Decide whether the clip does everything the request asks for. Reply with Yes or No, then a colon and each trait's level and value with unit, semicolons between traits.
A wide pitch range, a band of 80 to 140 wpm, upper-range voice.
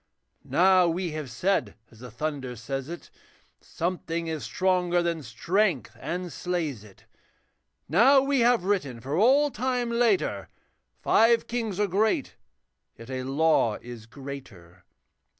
No: wide, 7.7 semitones; slow, 135 wpm; medium, 170 Hz